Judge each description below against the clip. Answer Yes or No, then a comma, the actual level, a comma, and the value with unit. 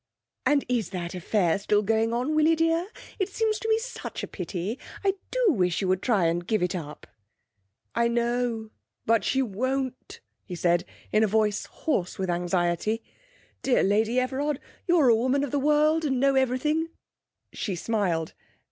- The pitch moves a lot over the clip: Yes, wide, 7.0 semitones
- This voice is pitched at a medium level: No, high, 235 Hz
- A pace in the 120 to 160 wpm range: No, average, 175 wpm